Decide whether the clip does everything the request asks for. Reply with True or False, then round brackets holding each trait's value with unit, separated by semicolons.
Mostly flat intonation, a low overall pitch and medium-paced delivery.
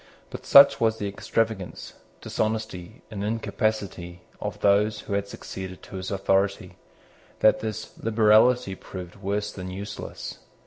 False (2.2 semitones; 100 Hz; 130 wpm)